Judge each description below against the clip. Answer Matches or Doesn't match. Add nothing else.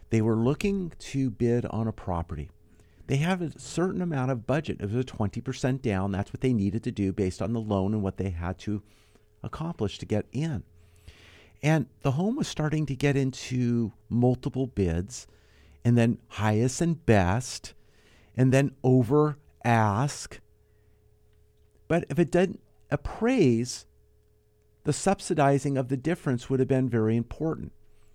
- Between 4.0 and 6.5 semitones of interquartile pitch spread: Matches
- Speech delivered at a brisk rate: Doesn't match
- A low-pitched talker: Matches